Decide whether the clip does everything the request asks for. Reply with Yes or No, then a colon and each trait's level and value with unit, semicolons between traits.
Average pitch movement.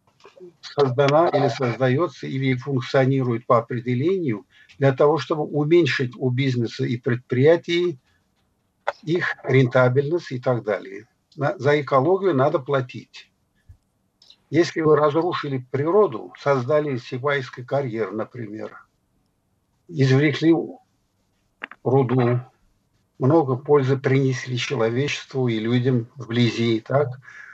Yes: average, 3.6 semitones